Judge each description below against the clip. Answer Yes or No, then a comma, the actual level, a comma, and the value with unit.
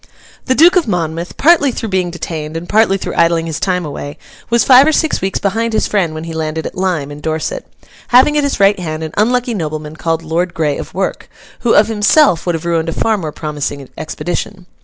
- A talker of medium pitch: Yes, medium, 175 Hz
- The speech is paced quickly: Yes, fast, 220 wpm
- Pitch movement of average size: No, wide, 5.8 semitones